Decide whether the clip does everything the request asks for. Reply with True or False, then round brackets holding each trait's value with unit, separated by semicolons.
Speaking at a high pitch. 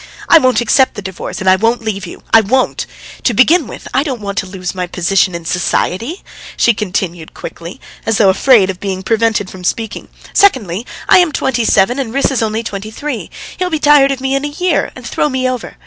True (225 Hz)